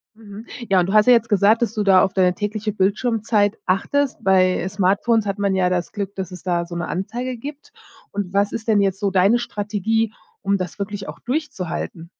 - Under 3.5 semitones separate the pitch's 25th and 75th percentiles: Yes, average, 2.8 semitones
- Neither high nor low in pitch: No, high, 200 Hz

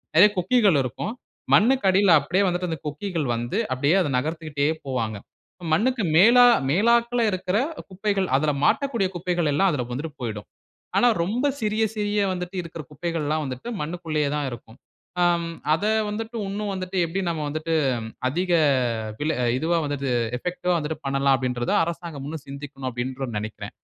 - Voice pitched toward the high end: No, medium, 165 Hz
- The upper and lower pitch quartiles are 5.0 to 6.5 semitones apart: Yes, wide, 5.6 semitones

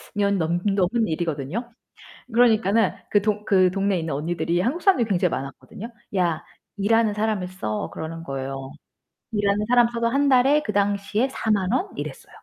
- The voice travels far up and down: No, average, 4.7 semitones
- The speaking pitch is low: No, high, 200 Hz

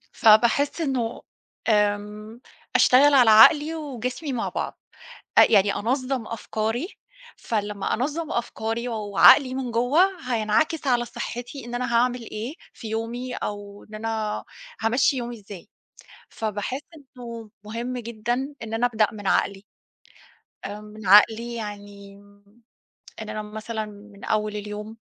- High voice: Yes, high, 225 Hz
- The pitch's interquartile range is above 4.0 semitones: No, average, 2.9 semitones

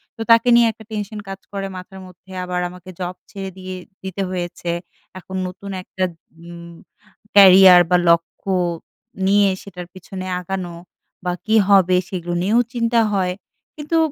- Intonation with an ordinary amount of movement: No, narrow, 1.9 semitones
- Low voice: No, high, 190 Hz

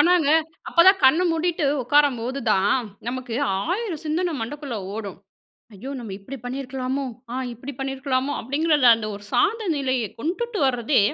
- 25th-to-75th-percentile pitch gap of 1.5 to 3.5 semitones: No, average, 4.7 semitones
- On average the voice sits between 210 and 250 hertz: No, very high, 270 Hz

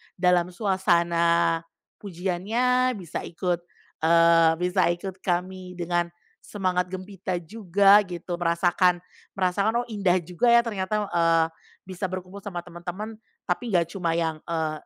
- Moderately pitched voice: Yes, medium, 180 Hz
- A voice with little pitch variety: Yes, narrow, 2.3 semitones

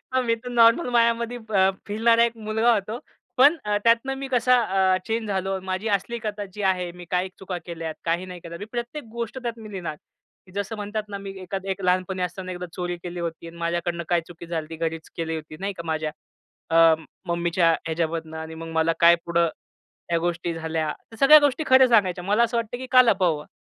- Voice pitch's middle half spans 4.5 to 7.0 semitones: Yes, average, 5.2 semitones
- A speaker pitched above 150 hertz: Yes, high, 190 Hz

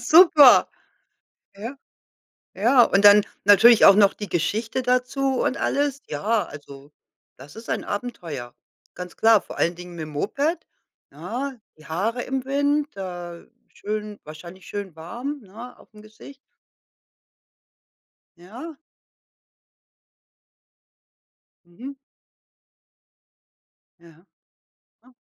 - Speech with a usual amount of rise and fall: No, wide, 6.3 semitones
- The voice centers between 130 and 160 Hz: No, high, 210 Hz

